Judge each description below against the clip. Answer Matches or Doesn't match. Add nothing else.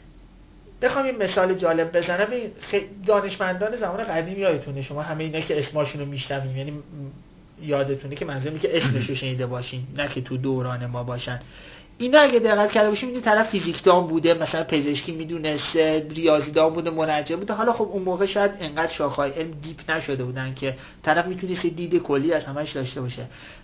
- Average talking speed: Doesn't match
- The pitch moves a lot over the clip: Doesn't match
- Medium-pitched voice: Matches